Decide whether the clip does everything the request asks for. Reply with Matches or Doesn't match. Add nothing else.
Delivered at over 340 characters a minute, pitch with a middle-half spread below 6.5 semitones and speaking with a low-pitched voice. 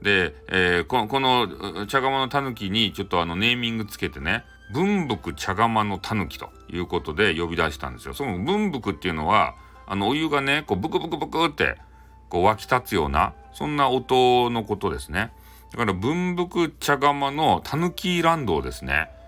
Doesn't match